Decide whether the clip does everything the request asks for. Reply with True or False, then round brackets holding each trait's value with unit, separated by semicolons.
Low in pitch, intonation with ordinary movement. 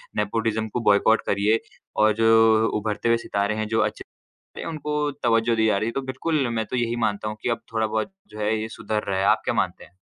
False (110 Hz; 1.5 semitones)